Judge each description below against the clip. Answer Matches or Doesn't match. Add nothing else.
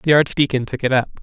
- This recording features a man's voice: Matches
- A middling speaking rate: Doesn't match